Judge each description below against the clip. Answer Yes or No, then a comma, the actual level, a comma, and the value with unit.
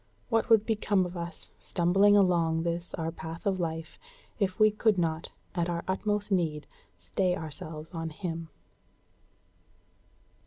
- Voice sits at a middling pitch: Yes, medium, 175 Hz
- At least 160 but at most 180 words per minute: No, average, 140 wpm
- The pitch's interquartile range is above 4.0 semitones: No, average, 3.4 semitones